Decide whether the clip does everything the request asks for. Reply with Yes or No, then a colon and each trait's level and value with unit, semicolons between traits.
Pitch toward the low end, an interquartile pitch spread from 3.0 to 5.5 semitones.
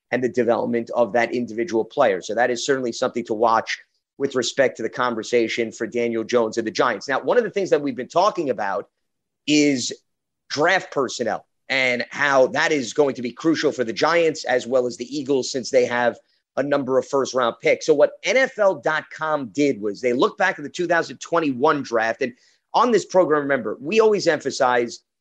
Yes: low, 130 Hz; average, 4.1 semitones